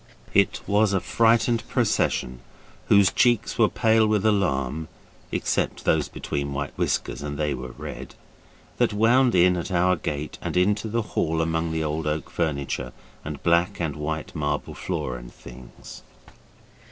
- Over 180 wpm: No, average, 155 wpm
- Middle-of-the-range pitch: No, very low, 80 Hz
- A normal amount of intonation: No, wide, 6.1 semitones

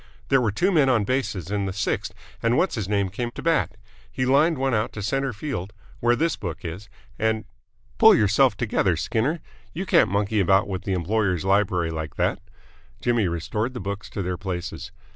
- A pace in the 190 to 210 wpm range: Yes, average, 200 wpm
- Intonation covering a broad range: No, average, 5.0 semitones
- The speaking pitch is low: Yes, low, 105 Hz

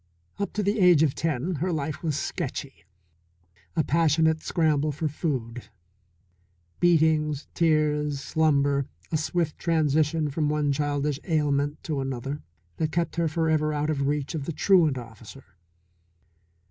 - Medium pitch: Yes, medium, 150 Hz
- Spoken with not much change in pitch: Yes, narrow, 2.2 semitones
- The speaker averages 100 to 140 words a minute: Yes, slow, 135 wpm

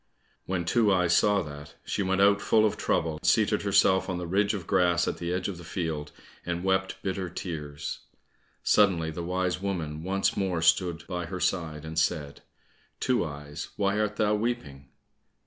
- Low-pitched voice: Yes, very low, 90 Hz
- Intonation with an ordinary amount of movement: Yes, average, 3.3 semitones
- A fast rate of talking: No, average, 180 wpm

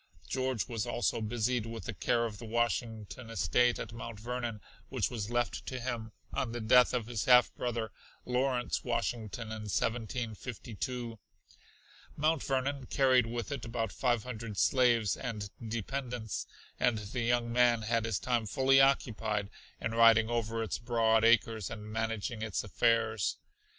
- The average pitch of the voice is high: No, low, 115 Hz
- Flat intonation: Yes, narrow, 1.9 semitones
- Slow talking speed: No, average, 150 wpm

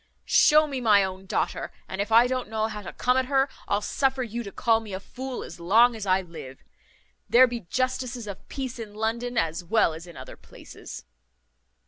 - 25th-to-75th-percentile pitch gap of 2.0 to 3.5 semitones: No, average, 4.4 semitones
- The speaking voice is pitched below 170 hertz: No, high, 225 Hz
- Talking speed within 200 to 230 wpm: Yes, fast, 205 wpm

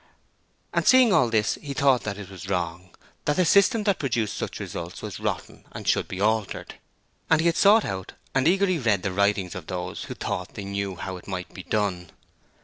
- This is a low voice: Yes, low, 105 Hz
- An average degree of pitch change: No, wide, 8.0 semitones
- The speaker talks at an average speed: No, fast, 210 wpm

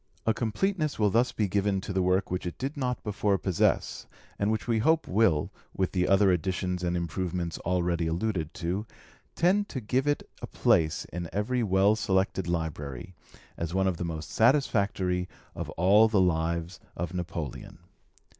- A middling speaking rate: Yes, average, 170 wpm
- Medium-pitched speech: No, very low, 95 Hz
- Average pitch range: Yes, average, 4.0 semitones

